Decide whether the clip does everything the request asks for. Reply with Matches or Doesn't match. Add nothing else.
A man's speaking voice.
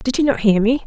Doesn't match